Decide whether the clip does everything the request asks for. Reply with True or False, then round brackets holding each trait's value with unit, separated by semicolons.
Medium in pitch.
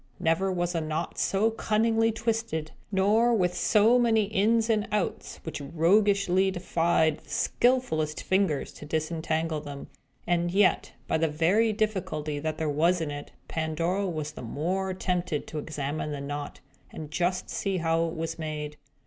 True (170 Hz)